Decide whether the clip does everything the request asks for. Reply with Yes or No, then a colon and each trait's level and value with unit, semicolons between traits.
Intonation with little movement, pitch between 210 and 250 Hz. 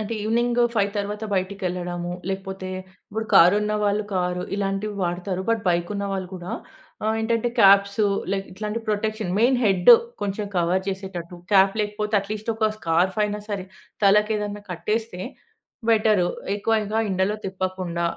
No: narrow, 2.3 semitones; high, 200 Hz